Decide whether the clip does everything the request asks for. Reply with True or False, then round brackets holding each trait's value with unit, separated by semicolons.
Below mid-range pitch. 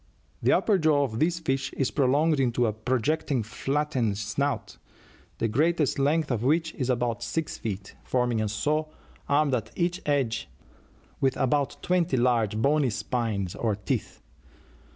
True (130 Hz)